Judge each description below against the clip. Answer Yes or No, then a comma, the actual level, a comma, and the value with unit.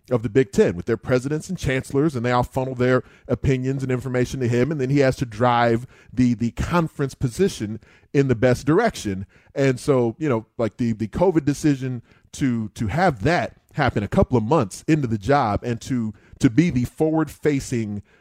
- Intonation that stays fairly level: No, average, 3.3 semitones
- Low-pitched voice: Yes, low, 125 Hz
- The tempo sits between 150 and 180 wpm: No, average, 200 wpm